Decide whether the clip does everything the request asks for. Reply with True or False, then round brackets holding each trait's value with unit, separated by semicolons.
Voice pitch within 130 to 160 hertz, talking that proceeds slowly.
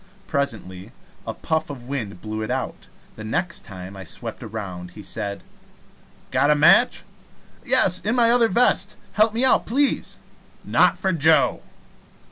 False (140 Hz; 150 wpm)